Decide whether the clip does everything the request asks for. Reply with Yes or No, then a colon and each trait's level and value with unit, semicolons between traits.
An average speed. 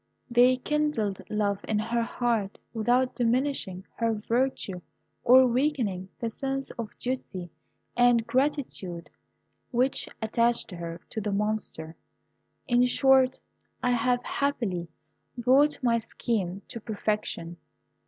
No: slow, 115 wpm